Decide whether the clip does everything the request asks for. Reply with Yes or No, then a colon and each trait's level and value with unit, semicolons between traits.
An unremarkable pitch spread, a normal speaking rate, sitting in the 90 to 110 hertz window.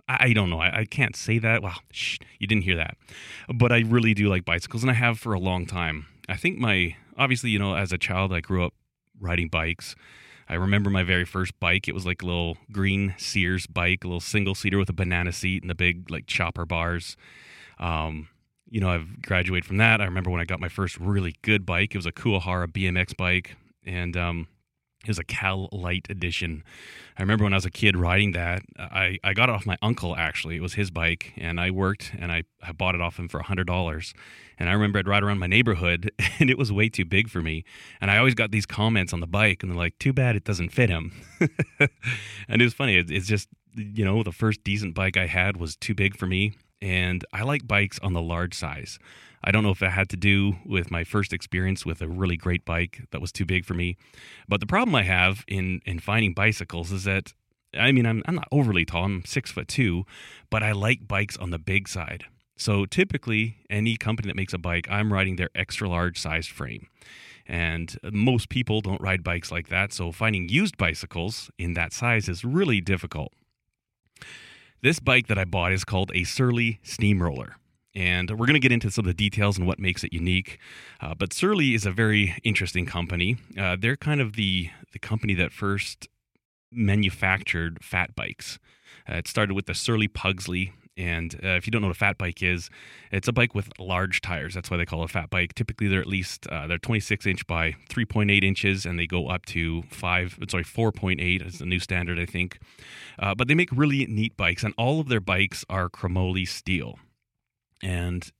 No: average, 3.3 semitones; fast, 220 wpm; very low, 95 Hz